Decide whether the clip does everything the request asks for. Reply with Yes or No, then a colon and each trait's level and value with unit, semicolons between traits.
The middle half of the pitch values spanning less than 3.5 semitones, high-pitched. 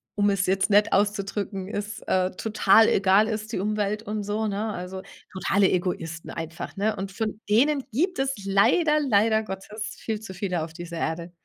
Yes: narrow, 2.5 semitones; high, 205 Hz